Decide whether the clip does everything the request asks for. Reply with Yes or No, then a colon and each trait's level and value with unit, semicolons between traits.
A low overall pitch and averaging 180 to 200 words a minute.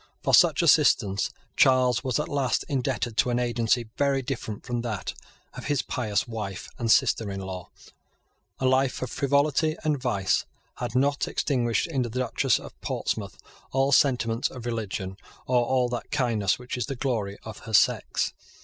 No: low, 125 Hz; average, 165 wpm